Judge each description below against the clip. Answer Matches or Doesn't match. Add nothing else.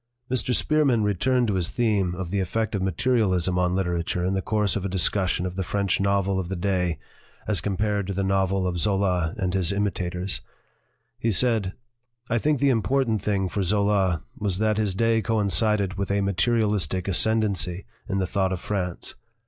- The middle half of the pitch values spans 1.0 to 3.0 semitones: Matches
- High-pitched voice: Doesn't match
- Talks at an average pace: Matches